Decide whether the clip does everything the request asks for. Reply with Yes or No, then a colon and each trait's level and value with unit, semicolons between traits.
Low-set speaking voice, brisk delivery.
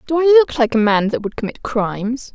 No: high, 235 Hz; fast, 255 wpm